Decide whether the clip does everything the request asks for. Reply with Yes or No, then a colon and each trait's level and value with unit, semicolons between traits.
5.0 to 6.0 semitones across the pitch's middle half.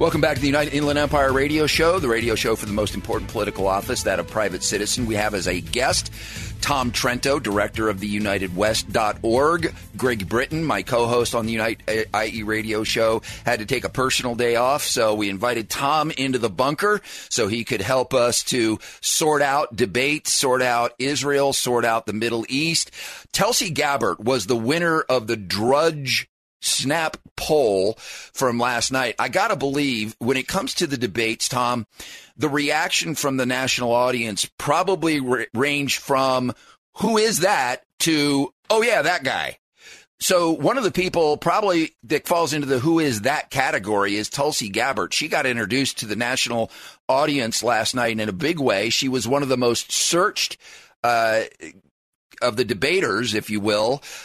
No: average, 4.5 semitones